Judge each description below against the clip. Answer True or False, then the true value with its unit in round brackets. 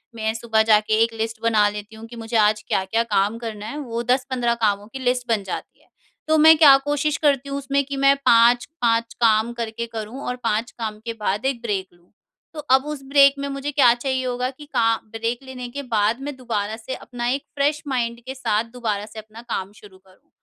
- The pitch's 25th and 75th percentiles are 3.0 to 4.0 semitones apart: True (3.5 semitones)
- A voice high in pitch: True (235 Hz)